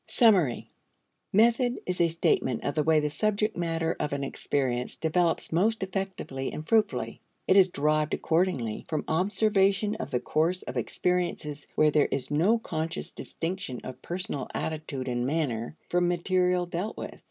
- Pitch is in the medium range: Yes, medium, 165 Hz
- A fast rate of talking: No, average, 155 wpm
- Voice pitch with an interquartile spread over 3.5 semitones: Yes, average, 4.2 semitones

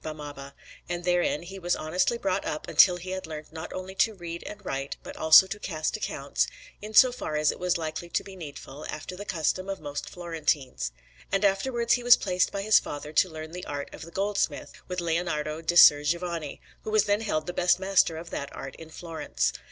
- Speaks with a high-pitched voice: No, medium, 175 Hz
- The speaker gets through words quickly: Yes, fast, 215 wpm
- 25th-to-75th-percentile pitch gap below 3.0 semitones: No, average, 3.7 semitones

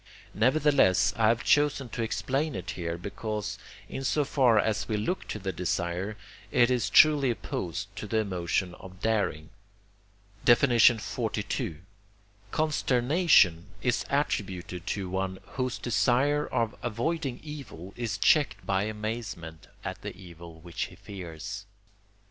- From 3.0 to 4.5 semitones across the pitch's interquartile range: No, average, 5.3 semitones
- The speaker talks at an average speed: No, slow, 130 wpm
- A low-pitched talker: Yes, low, 110 Hz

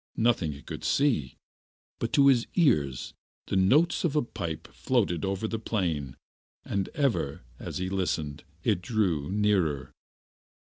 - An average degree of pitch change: No, wide, 7.2 semitones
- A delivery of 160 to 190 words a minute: No, average, 140 wpm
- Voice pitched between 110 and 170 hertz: No, very low, 95 Hz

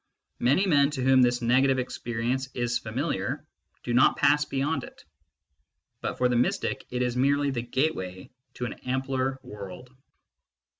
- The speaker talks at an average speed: Yes, average, 150 wpm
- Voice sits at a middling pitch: No, low, 130 Hz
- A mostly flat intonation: Yes, narrow, 1.9 semitones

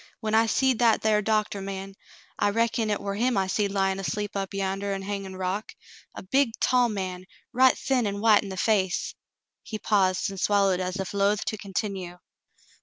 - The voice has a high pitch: Yes, high, 200 Hz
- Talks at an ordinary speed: No, fast, 220 wpm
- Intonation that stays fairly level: Yes, narrow, 2.1 semitones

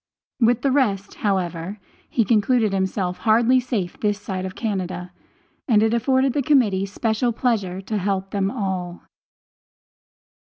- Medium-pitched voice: No, high, 205 Hz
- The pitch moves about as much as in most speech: Yes, average, 3.8 semitones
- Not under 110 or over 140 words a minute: Yes, slow, 135 wpm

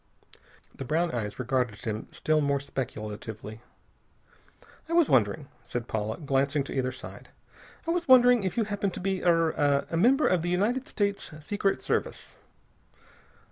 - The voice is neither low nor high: Yes, medium, 150 Hz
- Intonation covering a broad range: Yes, wide, 8.4 semitones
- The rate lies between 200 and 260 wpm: No, average, 155 wpm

